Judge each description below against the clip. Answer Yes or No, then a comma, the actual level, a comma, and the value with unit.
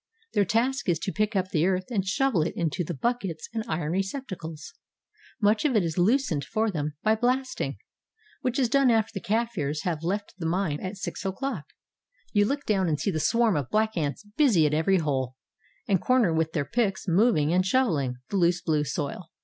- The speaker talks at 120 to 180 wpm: No, average, 200 wpm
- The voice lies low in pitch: No, high, 190 Hz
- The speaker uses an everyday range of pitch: No, wide, 5.8 semitones